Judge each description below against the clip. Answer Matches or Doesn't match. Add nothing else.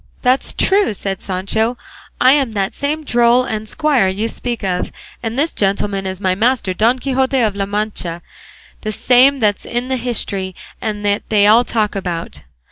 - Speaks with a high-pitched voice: Matches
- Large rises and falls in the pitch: Doesn't match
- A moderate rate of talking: Matches